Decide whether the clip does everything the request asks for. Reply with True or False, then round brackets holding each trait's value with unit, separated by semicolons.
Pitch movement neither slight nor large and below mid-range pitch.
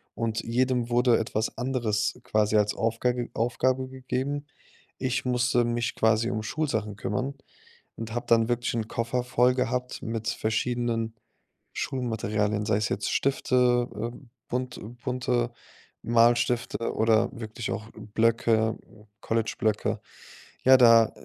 False (2.0 semitones; 115 Hz)